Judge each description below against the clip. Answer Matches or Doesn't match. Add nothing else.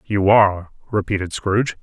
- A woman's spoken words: Doesn't match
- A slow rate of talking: Matches